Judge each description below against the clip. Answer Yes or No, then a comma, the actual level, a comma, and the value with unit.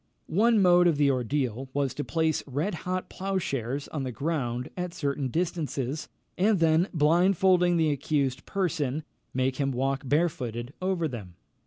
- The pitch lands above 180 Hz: No, medium, 150 Hz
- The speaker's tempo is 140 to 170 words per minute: Yes, average, 145 wpm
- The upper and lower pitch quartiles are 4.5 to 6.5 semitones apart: Yes, average, 4.8 semitones